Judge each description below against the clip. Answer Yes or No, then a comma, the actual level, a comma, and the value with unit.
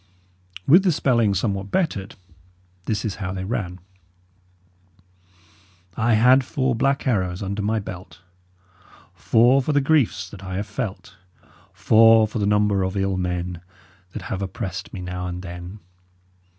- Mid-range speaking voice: No, low, 100 Hz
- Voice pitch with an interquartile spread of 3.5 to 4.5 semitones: Yes, average, 4.0 semitones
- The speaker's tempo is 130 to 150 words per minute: Yes, average, 145 wpm